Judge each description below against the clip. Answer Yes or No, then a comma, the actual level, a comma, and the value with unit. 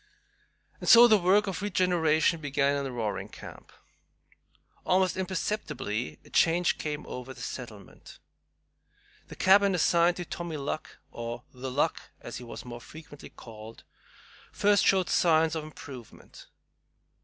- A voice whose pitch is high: No, medium, 155 Hz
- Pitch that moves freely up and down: Yes, wide, 6.4 semitones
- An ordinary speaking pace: No, slow, 130 wpm